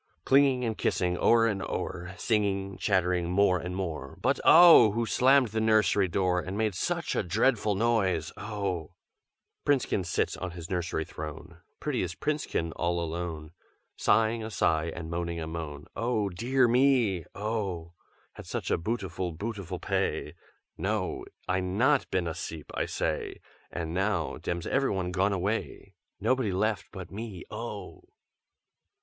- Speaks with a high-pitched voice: No, very low, 95 Hz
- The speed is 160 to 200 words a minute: No, average, 145 wpm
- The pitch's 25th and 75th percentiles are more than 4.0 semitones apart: Yes, average, 4.5 semitones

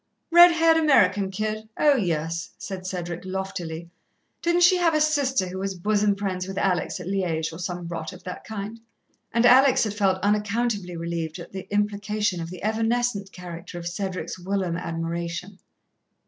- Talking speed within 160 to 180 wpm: Yes, average, 165 wpm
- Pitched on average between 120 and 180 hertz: No, high, 195 Hz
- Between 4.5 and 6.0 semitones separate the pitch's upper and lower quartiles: No, average, 3.7 semitones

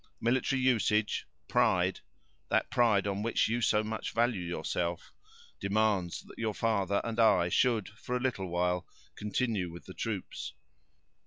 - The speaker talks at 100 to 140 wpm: Yes, slow, 135 wpm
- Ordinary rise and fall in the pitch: Yes, average, 3.7 semitones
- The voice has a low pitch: Yes, low, 105 Hz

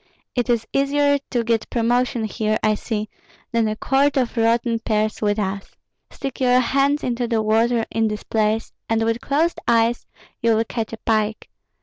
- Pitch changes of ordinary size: No, narrow, 2.2 semitones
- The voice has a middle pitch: No, high, 230 Hz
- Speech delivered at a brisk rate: No, average, 180 wpm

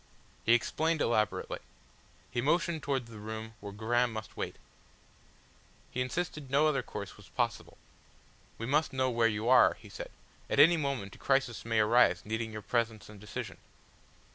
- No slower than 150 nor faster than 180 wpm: Yes, average, 165 wpm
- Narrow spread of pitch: No, average, 3.8 semitones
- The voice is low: Yes, low, 120 Hz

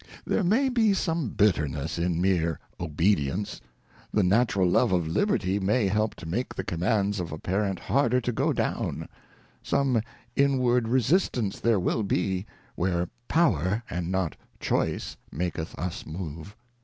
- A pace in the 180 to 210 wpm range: No, average, 145 wpm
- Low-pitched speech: Yes, very low, 95 Hz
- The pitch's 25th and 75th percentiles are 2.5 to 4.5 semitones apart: No, wide, 5.6 semitones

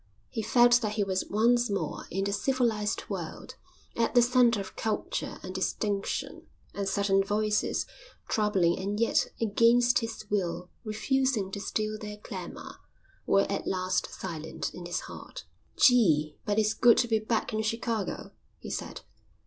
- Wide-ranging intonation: No, average, 2.9 semitones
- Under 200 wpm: Yes, average, 155 wpm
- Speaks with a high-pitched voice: Yes, high, 210 Hz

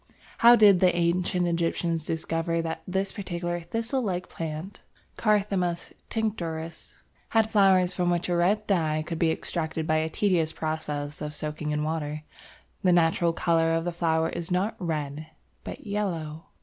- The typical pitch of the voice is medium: Yes, medium, 170 Hz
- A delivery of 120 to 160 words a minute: Yes, average, 155 wpm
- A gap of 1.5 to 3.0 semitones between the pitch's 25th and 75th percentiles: Yes, narrow, 2.6 semitones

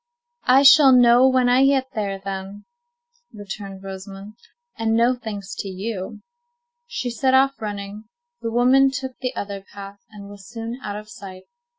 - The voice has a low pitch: No, high, 215 Hz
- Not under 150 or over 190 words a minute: Yes, average, 160 wpm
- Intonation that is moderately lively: Yes, average, 4.2 semitones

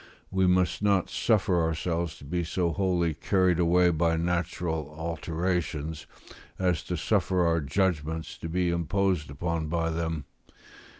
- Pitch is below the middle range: Yes, very low, 85 Hz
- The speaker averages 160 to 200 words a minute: No, slow, 135 wpm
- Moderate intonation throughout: No, narrow, 2.0 semitones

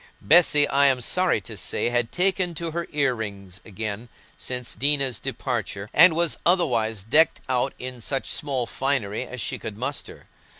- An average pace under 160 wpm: No, average, 165 wpm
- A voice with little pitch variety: No, average, 5.2 semitones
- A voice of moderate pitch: No, low, 130 Hz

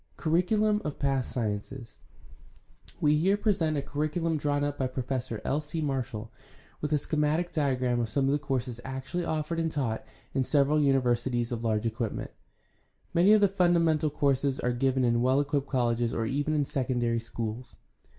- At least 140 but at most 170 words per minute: No, average, 180 wpm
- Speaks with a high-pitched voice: No, medium, 140 Hz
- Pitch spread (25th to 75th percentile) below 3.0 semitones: No, average, 4.0 semitones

